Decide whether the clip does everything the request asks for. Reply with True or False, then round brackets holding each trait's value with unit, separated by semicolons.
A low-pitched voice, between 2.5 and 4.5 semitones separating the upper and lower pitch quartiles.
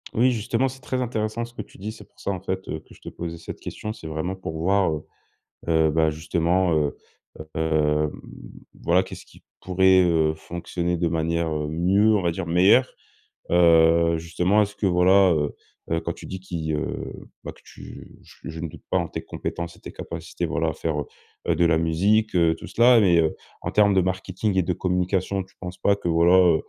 True (85 Hz; 2.9 semitones)